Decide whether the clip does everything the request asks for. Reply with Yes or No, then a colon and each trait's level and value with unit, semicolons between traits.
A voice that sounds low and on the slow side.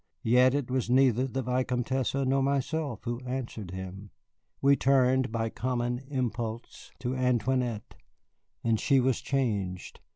Yes: low, 125 Hz; slow, 130 wpm